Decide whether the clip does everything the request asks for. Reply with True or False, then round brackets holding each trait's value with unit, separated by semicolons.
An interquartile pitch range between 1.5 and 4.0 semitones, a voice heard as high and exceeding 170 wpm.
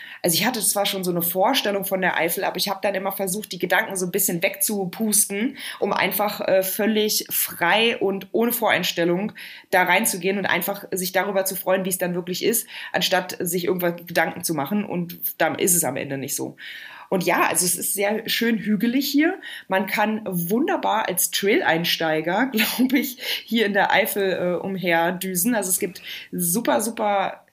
True (2.9 semitones; 195 Hz; 185 wpm)